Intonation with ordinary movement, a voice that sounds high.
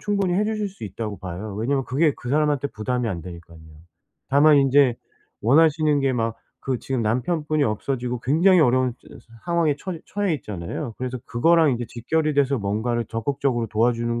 No: average, 5.0 semitones; low, 130 Hz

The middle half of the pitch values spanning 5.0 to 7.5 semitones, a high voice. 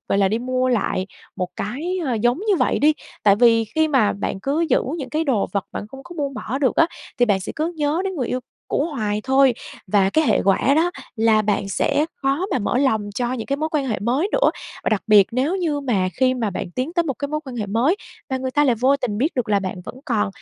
Yes: average, 5.3 semitones; very high, 255 Hz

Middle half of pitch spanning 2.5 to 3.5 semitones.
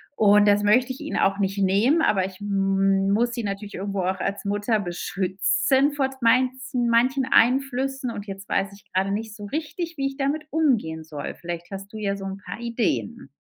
No: average, 4.8 semitones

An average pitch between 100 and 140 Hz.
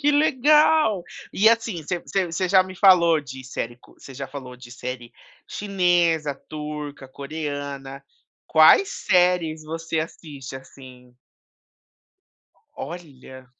No: medium, 155 Hz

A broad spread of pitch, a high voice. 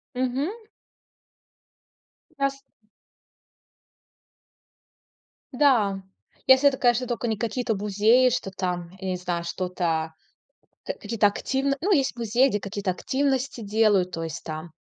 Yes: wide, 5.7 semitones; high, 220 Hz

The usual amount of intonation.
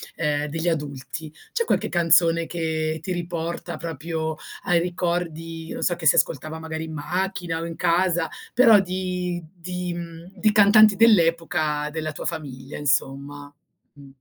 No: narrow, 2.1 semitones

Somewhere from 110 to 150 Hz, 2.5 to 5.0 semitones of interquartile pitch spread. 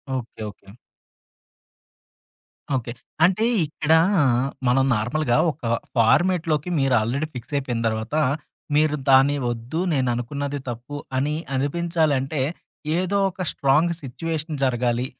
Yes: medium, 140 Hz; average, 4.3 semitones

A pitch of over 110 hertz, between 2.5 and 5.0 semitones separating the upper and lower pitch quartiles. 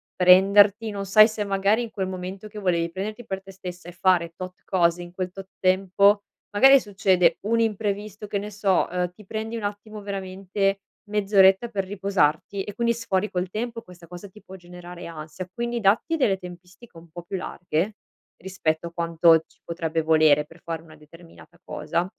Yes: high, 190 Hz; average, 2.8 semitones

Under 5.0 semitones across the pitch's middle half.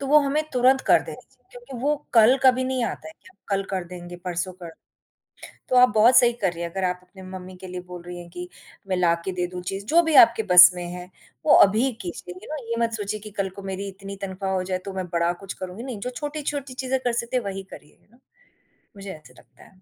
No: wide, 5.5 semitones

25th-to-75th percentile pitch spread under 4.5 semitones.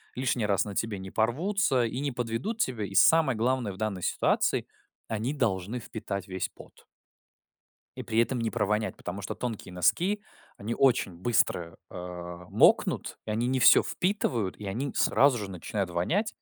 No: average, 4.9 semitones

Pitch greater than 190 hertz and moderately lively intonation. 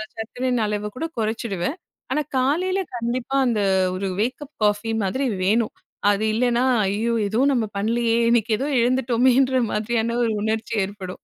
Yes: high, 230 Hz; average, 3.2 semitones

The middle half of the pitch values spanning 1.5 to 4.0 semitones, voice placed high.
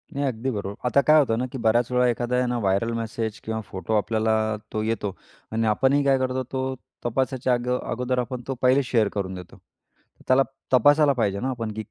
No: average, 3.0 semitones; low, 120 Hz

